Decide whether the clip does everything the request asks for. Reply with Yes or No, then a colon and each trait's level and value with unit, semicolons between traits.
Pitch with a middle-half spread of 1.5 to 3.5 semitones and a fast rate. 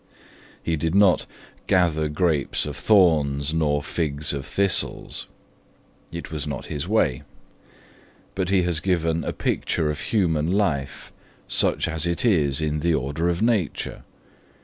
No: average, 3.2 semitones; average, 140 wpm